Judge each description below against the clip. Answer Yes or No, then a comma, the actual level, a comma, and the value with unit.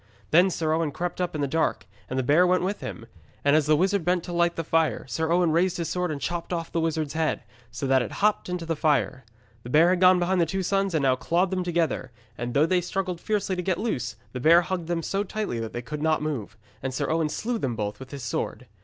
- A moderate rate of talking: No, fast, 260 wpm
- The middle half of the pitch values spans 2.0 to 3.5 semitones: No, average, 4.0 semitones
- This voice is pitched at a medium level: Yes, medium, 165 Hz